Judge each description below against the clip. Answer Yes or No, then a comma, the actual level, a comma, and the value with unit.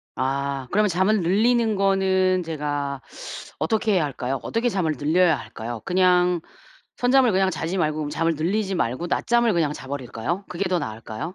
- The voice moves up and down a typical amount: Yes, average, 5.0 semitones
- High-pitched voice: No, medium, 175 Hz